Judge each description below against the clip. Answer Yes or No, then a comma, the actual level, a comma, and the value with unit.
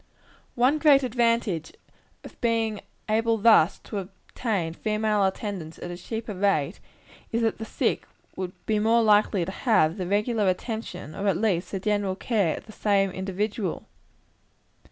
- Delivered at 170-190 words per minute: No, average, 155 wpm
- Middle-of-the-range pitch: No, high, 210 Hz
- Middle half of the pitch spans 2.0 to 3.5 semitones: Yes, average, 3.1 semitones